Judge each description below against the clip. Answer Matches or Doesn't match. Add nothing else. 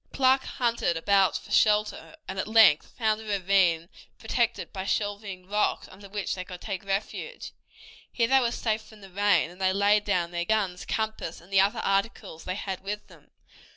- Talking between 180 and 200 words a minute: Matches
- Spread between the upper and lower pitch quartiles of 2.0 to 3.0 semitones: Matches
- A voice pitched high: Matches